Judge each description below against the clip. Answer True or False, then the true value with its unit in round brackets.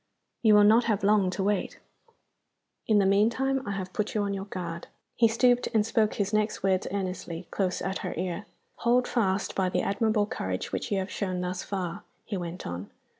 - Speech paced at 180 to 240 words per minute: True (200 wpm)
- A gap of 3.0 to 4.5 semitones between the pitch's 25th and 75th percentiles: False (2.6 semitones)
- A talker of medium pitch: False (200 Hz)